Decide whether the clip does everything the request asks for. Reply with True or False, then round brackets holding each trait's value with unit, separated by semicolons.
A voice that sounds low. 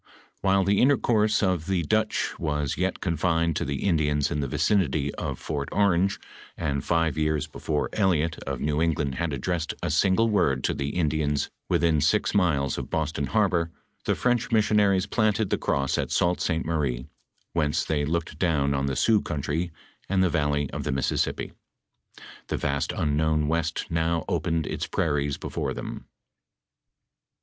True (80 Hz)